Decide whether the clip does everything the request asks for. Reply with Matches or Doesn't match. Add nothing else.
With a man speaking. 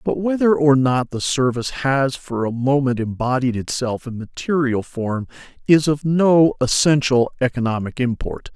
Matches